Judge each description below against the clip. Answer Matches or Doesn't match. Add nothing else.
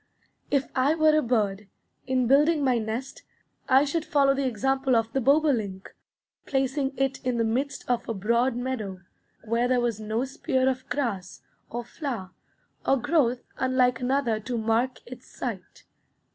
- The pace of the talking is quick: Doesn't match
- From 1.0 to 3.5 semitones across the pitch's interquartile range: Matches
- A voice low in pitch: Doesn't match